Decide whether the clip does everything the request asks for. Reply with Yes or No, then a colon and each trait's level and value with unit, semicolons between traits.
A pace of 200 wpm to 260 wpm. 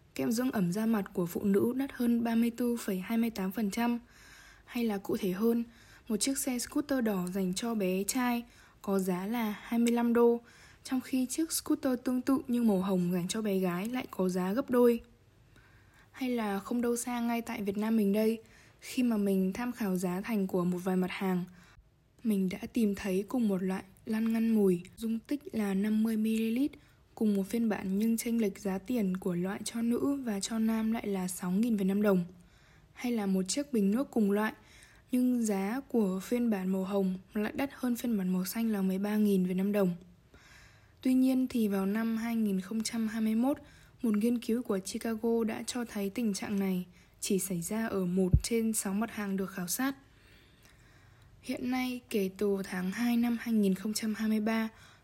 No: average, 185 wpm